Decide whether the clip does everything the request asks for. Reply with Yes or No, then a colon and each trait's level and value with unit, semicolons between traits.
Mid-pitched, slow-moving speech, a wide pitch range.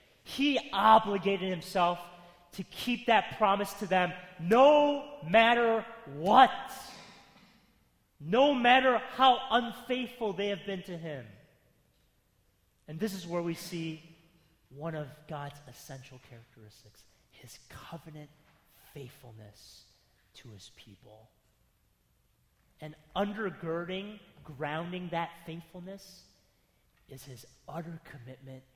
Yes: medium, 170 Hz; slow, 100 wpm; wide, 6.6 semitones